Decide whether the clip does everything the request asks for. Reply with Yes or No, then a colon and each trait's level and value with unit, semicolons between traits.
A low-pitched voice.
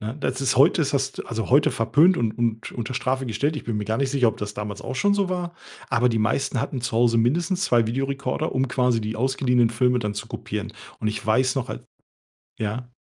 Yes: low, 125 Hz